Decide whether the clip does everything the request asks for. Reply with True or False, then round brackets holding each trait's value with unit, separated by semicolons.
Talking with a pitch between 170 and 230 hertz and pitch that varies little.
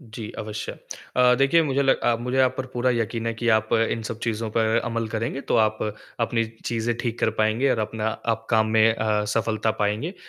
False (115 Hz; 2.2 semitones)